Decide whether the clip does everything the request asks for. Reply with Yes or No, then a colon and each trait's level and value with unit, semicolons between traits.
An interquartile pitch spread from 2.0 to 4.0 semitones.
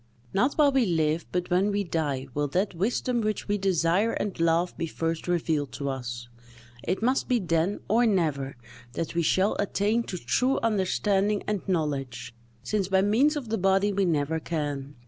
No: average, 4.8 semitones